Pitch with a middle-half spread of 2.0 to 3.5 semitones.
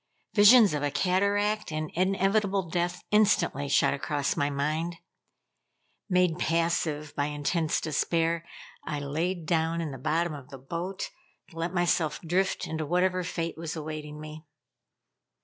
Yes: average, 3.2 semitones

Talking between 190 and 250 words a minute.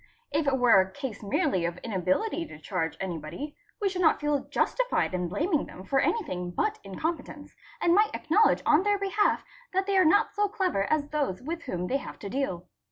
Yes: average, 200 wpm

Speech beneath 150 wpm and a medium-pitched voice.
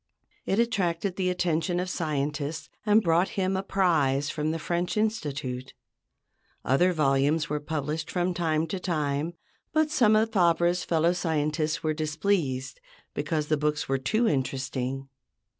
Yes: average, 140 wpm; medium, 160 Hz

